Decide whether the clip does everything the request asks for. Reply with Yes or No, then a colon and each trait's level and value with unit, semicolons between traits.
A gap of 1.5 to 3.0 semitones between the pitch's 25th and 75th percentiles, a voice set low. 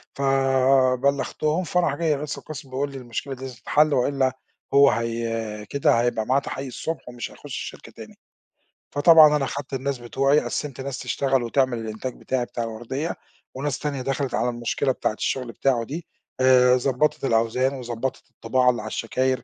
Yes: narrow, 2.4 semitones; low, 130 Hz